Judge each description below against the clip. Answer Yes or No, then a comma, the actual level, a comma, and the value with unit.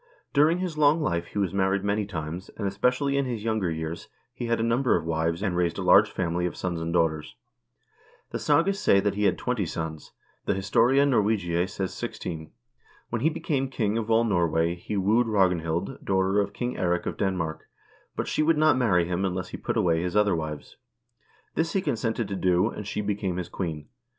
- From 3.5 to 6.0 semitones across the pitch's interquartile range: Yes, average, 4.9 semitones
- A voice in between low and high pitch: No, low, 100 Hz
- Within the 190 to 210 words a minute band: Yes, fast, 205 wpm